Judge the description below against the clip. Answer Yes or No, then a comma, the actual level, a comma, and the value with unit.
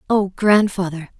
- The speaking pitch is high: Yes, high, 195 Hz